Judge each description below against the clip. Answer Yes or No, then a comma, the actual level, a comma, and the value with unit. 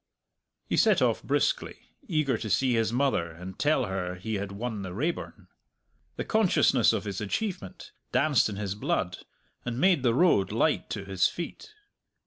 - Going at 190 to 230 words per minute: No, average, 165 wpm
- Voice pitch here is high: No, low, 110 Hz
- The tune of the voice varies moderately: No, wide, 6.6 semitones